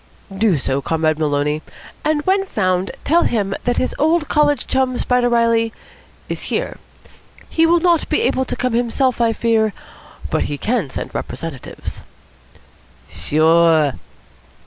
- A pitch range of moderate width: No, wide, 8.5 semitones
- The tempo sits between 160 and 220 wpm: No, average, 140 wpm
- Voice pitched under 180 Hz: No, high, 230 Hz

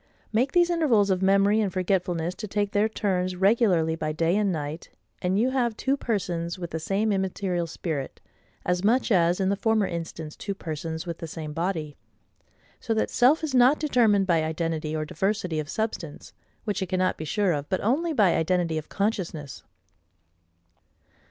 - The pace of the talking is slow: No, average, 175 wpm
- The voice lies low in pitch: No, medium, 185 Hz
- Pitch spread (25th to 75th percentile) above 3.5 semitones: Yes, average, 4.4 semitones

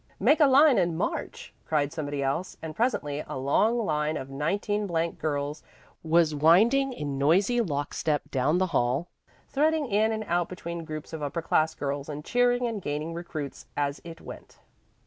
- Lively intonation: Yes, wide, 6.1 semitones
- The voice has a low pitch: No, medium, 165 Hz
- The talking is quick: No, average, 170 wpm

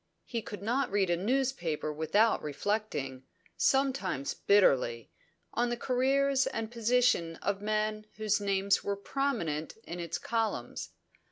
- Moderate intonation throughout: No, wide, 6.0 semitones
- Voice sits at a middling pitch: No, high, 215 Hz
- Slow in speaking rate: Yes, slow, 125 wpm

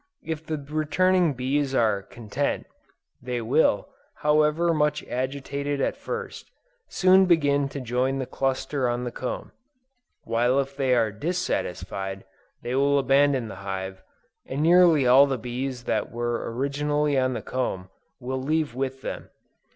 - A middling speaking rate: Yes, average, 145 wpm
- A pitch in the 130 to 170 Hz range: Yes, low, 135 Hz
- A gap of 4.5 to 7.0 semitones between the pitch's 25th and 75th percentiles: No, average, 3.3 semitones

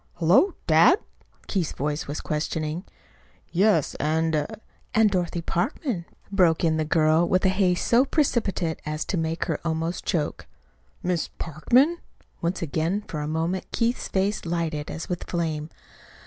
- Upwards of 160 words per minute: No, average, 150 wpm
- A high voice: No, medium, 170 Hz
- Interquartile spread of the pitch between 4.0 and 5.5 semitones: No, average, 3.2 semitones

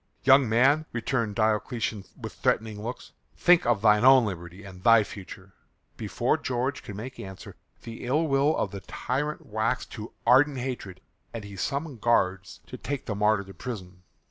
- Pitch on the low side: Yes, low, 115 Hz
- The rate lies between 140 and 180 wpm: Yes, average, 170 wpm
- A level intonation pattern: No, average, 4.5 semitones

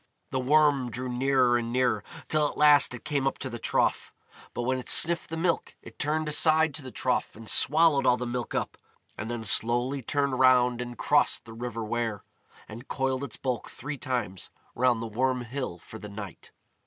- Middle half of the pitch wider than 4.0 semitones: No, average, 2.9 semitones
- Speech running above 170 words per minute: Yes, average, 200 wpm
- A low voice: Yes, low, 125 Hz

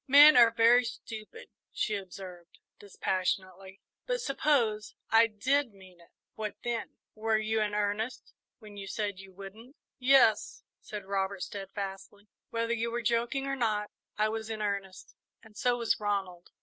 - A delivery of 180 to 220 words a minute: No, average, 150 wpm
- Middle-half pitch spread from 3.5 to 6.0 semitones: No, average, 2.9 semitones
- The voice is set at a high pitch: Yes, high, 215 Hz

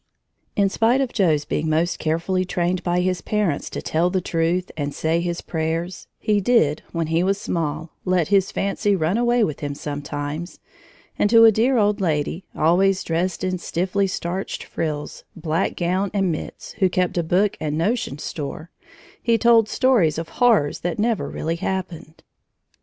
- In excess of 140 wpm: Yes, average, 170 wpm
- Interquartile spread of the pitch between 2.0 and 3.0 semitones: No, average, 3.6 semitones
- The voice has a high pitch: No, medium, 180 Hz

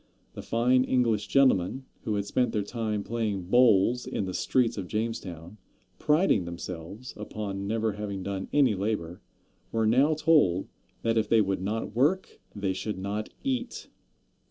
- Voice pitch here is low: Yes, low, 110 Hz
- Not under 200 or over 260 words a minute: No, average, 155 wpm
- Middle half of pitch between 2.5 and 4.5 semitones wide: Yes, average, 3.9 semitones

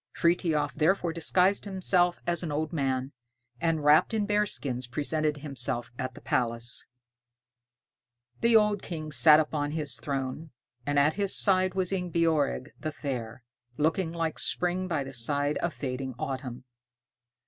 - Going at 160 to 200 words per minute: No, average, 140 wpm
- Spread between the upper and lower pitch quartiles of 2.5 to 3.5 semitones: No, average, 4.3 semitones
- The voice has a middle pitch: Yes, medium, 155 Hz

